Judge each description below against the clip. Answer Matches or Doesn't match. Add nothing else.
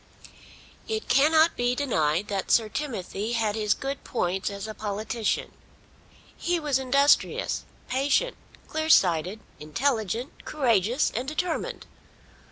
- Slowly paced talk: Matches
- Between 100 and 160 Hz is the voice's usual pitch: Doesn't match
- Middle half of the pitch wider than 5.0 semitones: Matches